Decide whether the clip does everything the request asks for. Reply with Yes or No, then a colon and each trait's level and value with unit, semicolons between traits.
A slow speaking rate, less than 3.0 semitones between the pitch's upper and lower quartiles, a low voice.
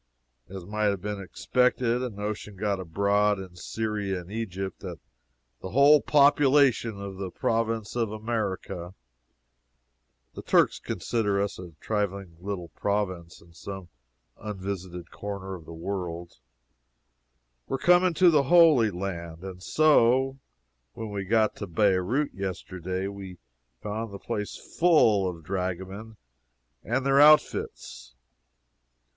No: slow, 125 wpm; average, 3.6 semitones; low, 100 Hz